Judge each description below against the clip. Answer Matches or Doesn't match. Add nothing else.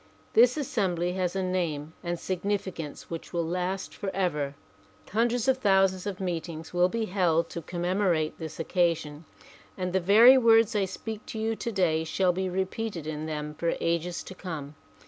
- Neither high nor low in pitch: Matches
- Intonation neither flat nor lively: Matches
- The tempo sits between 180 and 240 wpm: Doesn't match